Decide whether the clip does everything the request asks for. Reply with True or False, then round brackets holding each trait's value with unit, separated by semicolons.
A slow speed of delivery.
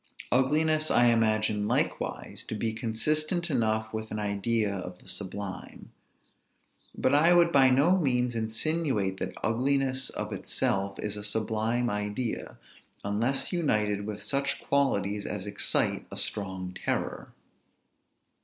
True (125 wpm)